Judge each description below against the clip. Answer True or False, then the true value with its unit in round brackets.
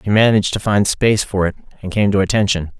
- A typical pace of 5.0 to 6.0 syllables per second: False (6.6 syllables/s)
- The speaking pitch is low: True (100 Hz)